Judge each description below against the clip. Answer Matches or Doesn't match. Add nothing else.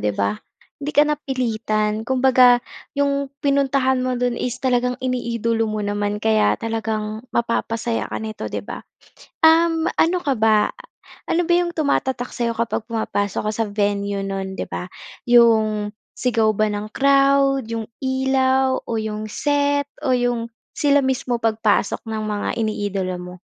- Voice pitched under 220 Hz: Doesn't match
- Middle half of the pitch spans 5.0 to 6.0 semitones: Doesn't match